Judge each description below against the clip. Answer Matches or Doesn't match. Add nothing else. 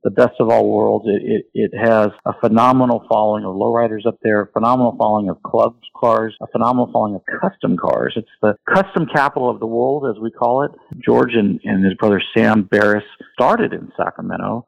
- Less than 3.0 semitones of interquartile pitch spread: Matches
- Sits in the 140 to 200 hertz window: Doesn't match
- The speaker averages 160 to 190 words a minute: Doesn't match